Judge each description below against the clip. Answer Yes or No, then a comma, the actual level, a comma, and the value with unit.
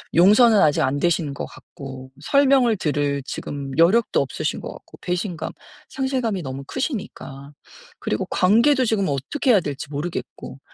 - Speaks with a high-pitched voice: No, medium, 175 Hz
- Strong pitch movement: Yes, wide, 8.5 semitones